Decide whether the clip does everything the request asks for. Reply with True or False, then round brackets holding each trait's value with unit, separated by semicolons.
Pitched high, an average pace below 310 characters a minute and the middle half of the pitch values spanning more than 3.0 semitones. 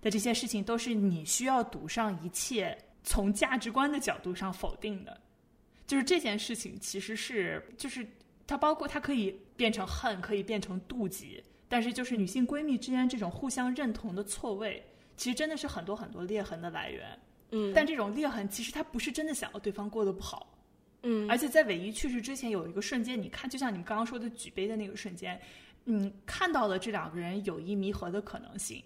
False (225 Hz; 320 characters per minute; 3.9 semitones)